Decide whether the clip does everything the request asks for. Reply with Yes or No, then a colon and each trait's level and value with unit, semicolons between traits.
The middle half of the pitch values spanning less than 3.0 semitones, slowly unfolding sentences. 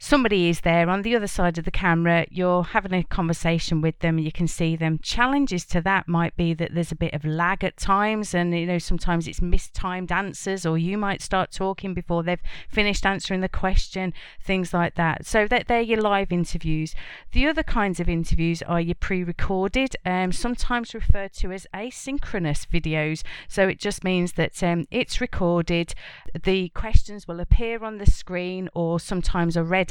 No: narrow, 2.6 semitones; average, 190 wpm